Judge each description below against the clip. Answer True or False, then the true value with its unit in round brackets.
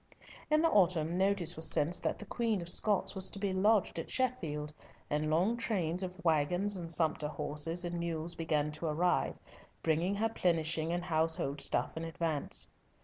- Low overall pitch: False (170 Hz)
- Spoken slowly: False (175 wpm)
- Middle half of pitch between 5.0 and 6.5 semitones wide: False (3.3 semitones)